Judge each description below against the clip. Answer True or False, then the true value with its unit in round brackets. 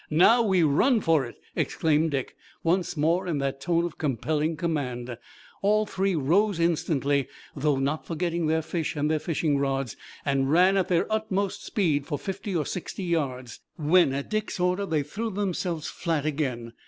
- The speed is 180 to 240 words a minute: False (170 wpm)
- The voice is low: False (160 Hz)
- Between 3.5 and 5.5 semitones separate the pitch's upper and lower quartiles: True (4.3 semitones)